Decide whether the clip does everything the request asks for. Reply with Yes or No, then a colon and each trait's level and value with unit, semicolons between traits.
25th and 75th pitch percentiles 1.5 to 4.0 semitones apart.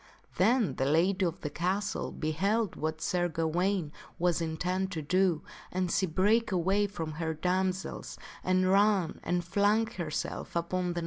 Yes: average, 2.9 semitones